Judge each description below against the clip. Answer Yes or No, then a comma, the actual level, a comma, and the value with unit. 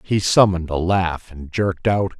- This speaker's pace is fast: No, average, 190 wpm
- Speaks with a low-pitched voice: Yes, very low, 90 Hz